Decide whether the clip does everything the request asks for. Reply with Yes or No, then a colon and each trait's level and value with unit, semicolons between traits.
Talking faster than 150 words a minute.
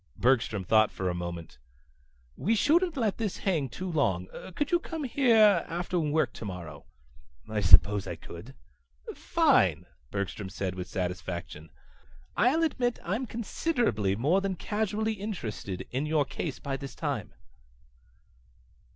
No: slow, 135 wpm